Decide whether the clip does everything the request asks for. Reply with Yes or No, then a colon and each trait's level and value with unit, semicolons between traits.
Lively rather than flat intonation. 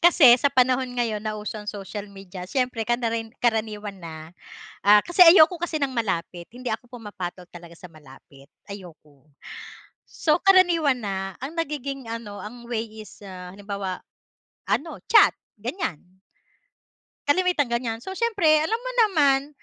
Yes: wide, 6.1 semitones